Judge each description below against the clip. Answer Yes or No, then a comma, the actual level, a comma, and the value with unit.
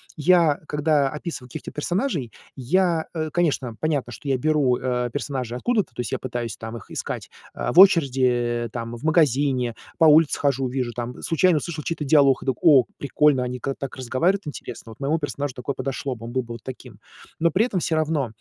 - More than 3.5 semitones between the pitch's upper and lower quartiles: Yes, average, 4.2 semitones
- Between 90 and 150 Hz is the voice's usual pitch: Yes, medium, 140 Hz